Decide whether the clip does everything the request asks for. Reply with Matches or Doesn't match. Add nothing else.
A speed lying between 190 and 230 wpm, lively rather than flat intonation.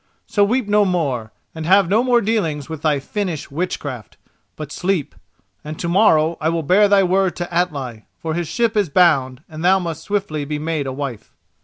Doesn't match